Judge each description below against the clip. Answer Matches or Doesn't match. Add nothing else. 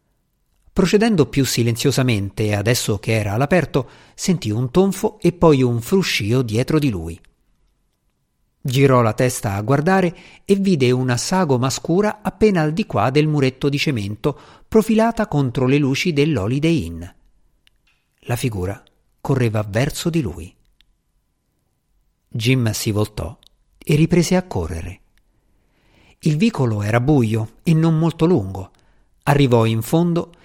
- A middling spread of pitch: Doesn't match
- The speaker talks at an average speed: Matches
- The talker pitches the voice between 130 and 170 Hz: Matches